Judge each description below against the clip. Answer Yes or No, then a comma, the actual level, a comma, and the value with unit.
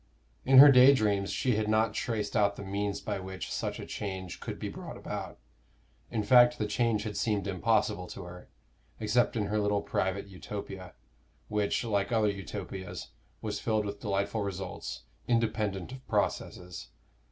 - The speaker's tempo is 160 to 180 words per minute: Yes, average, 165 wpm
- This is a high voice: No, low, 105 Hz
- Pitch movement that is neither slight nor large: No, narrow, 2.2 semitones